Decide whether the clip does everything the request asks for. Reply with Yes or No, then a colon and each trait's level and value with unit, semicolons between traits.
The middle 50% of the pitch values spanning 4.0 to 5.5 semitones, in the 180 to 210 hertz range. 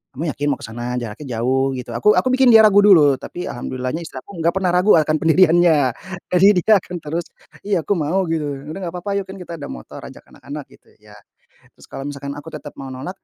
No: average, 4.9 semitones; medium, 160 Hz